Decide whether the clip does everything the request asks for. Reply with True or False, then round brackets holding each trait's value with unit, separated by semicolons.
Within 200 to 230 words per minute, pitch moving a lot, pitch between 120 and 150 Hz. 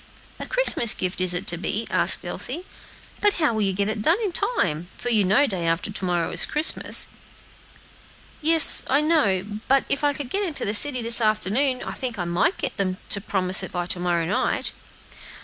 False (205 wpm; 7.7 semitones; 215 Hz)